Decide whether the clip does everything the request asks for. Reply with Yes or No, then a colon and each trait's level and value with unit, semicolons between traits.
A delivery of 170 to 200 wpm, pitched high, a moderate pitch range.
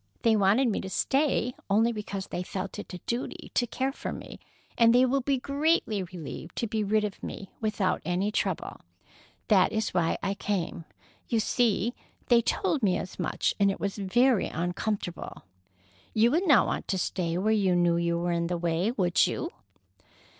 Yes: average, 185 wpm; high, 205 Hz; average, 4.6 semitones